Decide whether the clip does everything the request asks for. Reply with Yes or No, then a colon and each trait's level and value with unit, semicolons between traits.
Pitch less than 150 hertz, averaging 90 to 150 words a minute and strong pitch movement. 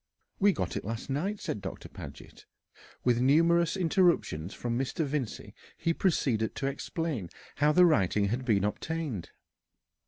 Yes: low, 135 Hz; average, 145 wpm; wide, 6.9 semitones